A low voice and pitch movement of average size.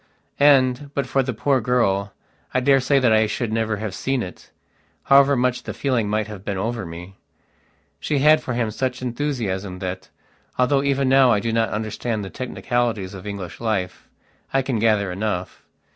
Yes: low, 115 Hz; average, 4.3 semitones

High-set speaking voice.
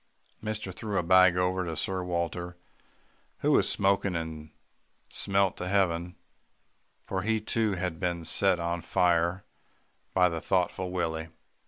No: very low, 90 Hz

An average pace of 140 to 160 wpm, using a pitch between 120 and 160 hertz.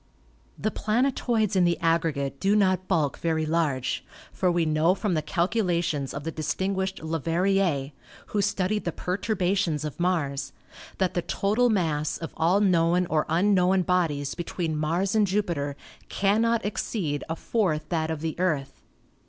No: average, 150 wpm; medium, 175 Hz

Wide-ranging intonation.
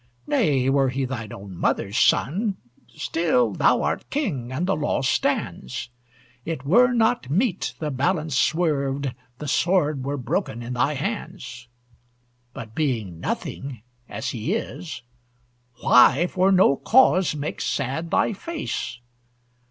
Yes: wide, 6.2 semitones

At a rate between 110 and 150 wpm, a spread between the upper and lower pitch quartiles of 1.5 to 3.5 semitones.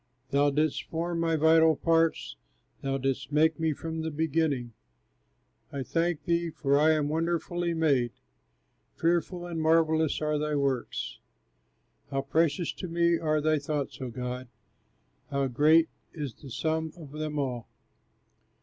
Yes: average, 140 wpm; average, 2.8 semitones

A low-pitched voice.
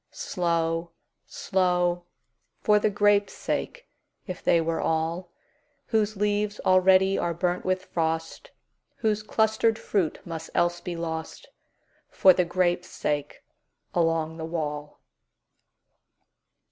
No: medium, 175 Hz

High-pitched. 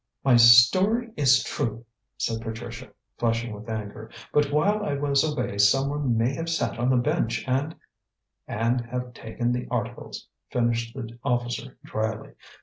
No: low, 120 Hz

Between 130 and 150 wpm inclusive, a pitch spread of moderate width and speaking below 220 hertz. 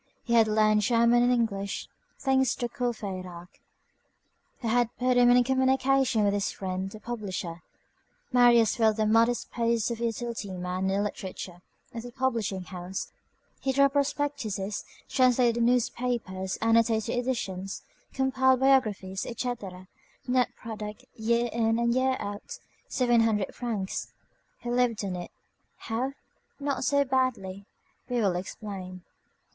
No: slow, 135 wpm; average, 3.7 semitones; high, 230 Hz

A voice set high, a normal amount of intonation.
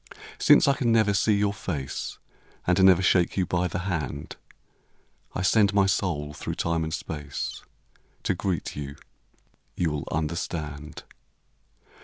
No: very low, 90 Hz; average, 4.3 semitones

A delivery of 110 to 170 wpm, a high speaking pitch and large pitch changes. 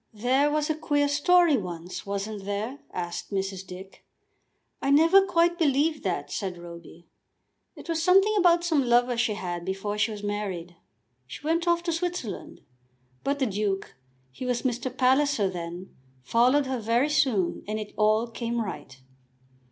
Yes: average, 160 wpm; high, 235 Hz; wide, 7.3 semitones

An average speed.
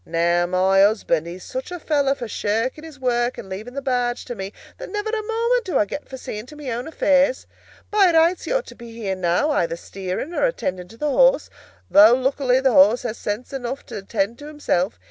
No: fast, 225 wpm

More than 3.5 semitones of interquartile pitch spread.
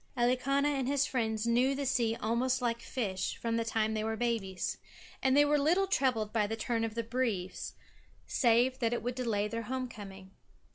No: average, 2.8 semitones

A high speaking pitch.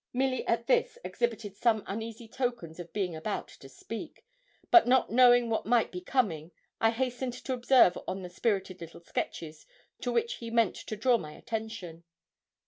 Yes: high, 225 Hz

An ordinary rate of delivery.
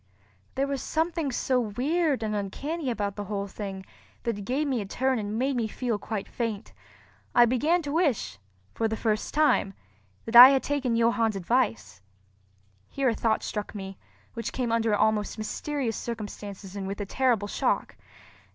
Yes: average, 170 wpm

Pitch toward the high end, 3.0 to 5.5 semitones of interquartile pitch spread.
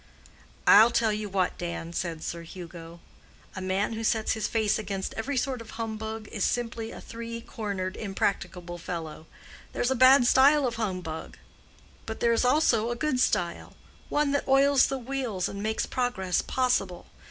Yes: high, 220 Hz; average, 4.8 semitones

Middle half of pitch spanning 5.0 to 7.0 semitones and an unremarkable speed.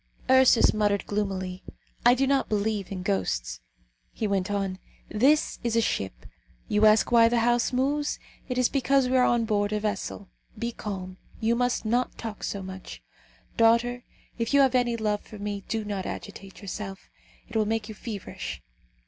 No: average, 3.2 semitones; average, 175 wpm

